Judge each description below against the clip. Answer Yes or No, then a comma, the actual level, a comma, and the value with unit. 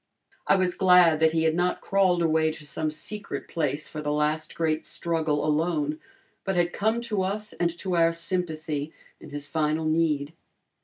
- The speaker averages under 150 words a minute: No, average, 175 wpm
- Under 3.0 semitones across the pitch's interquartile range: Yes, narrow, 2.5 semitones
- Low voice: No, medium, 160 Hz